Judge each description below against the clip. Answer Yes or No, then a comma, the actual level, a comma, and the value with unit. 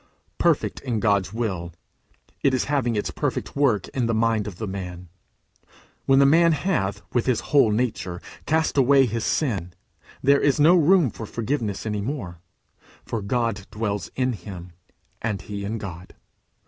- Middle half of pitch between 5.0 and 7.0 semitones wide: Yes, average, 5.3 semitones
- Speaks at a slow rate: No, average, 160 wpm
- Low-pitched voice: Yes, low, 115 Hz